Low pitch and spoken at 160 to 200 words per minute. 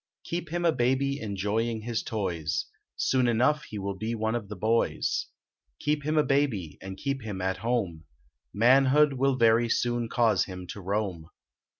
Yes: low, 115 Hz; average, 170 wpm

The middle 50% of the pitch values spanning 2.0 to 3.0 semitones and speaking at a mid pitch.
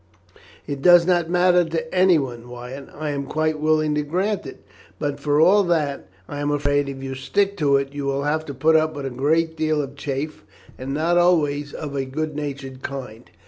Yes: average, 2.7 semitones; medium, 145 Hz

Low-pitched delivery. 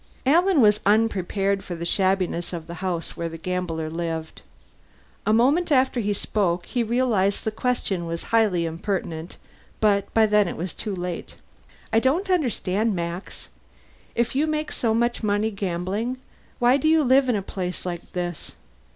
No: high, 205 Hz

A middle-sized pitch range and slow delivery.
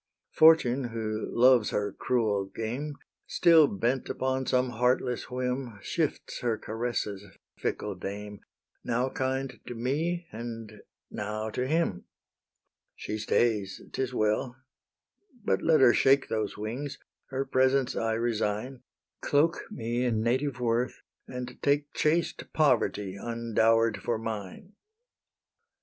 Yes: average, 3.3 semitones; slow, 120 wpm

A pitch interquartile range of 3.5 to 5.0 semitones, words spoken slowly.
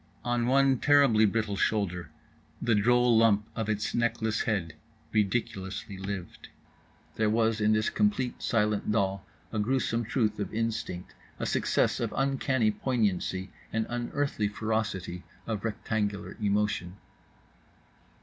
No: narrow, 2.6 semitones; slow, 120 wpm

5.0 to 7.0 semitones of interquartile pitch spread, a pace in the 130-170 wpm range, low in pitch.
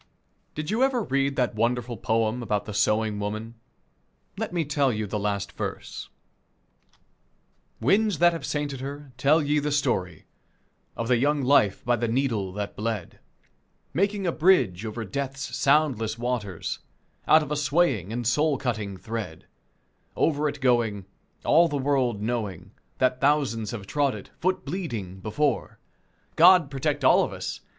Yes: wide, 5.4 semitones; average, 155 wpm; low, 125 Hz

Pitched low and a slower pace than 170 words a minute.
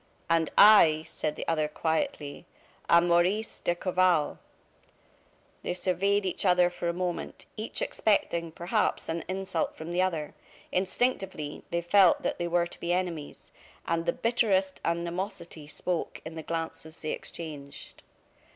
No: medium, 175 Hz; average, 140 wpm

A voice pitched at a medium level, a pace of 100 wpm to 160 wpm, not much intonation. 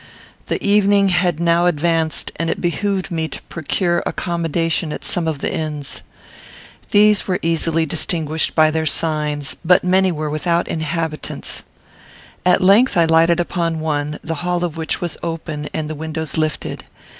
Yes: medium, 165 Hz; average, 155 wpm; narrow, 2.0 semitones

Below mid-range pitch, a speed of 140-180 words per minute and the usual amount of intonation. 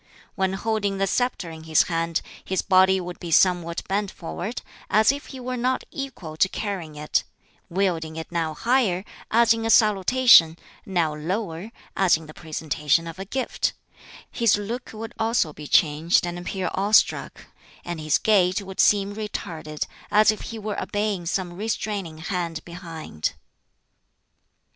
No: high, 190 Hz; average, 155 wpm; average, 4.5 semitones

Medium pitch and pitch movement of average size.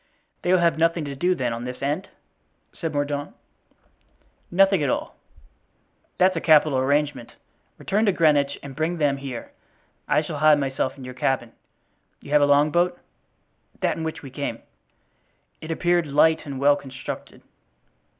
Yes: medium, 145 Hz; average, 3.2 semitones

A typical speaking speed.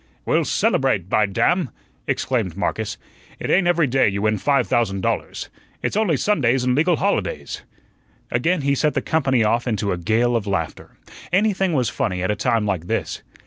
Yes: average, 180 wpm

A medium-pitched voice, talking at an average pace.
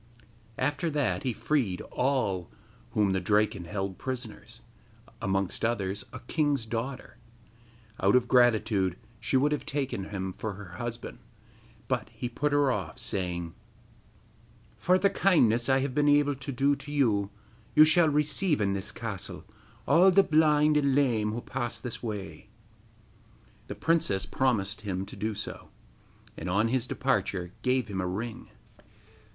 No: low, 120 Hz; average, 150 wpm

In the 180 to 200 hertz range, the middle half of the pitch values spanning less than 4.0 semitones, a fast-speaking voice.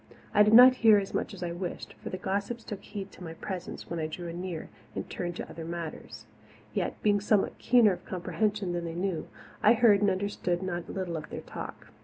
Yes: high, 190 Hz; average, 3.1 semitones; fast, 225 wpm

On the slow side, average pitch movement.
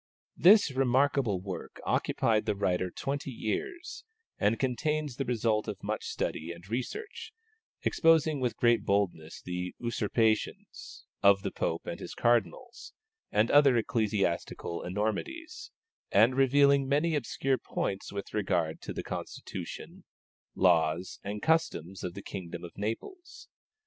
No: slow, 130 wpm; wide, 6.5 semitones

